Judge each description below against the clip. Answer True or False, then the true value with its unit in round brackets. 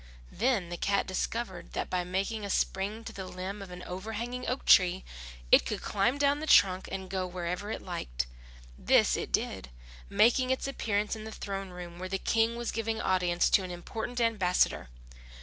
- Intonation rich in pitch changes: False (3.7 semitones)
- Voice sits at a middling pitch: False (195 Hz)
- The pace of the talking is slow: False (185 wpm)